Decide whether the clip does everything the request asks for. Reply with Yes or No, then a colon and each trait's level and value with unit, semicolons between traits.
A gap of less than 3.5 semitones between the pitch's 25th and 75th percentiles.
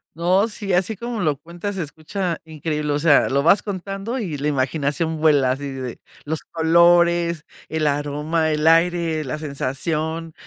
Yes: average, 2.8 semitones